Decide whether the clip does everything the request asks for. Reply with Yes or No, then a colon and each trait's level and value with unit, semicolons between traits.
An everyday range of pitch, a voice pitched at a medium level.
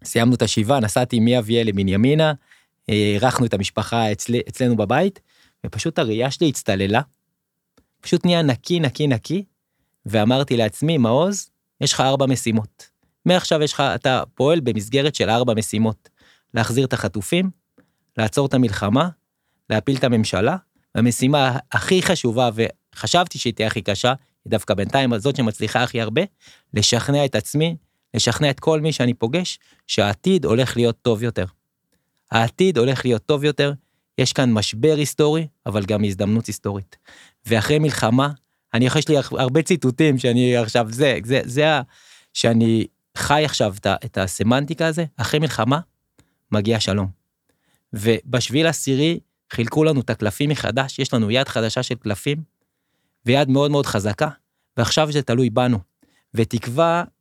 No: average, 4.7 semitones; low, 125 Hz